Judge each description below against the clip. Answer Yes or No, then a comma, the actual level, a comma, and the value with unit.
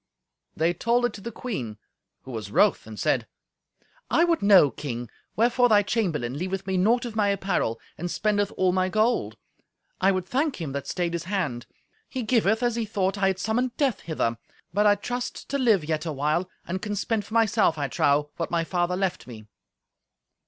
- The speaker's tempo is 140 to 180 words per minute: No, average, 195 wpm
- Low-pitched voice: No, high, 190 Hz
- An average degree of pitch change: No, wide, 5.7 semitones